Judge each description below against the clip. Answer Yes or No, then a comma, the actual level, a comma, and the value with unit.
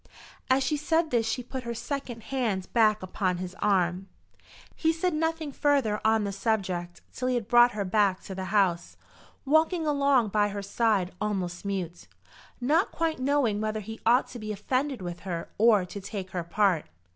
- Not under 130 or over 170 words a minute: No, average, 180 wpm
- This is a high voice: Yes, high, 215 Hz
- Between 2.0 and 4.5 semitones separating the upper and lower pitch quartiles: No, wide, 5.4 semitones